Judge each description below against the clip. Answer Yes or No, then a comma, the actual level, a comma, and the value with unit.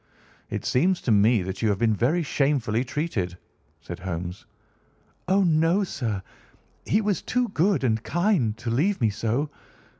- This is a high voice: No, low, 125 Hz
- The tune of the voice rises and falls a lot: Yes, wide, 8.1 semitones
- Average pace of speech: Yes, average, 155 wpm